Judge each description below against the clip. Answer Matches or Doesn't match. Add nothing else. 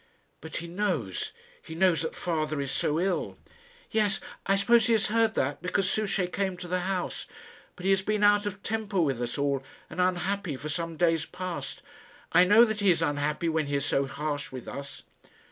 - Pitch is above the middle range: Doesn't match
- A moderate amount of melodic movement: Matches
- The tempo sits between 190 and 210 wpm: Matches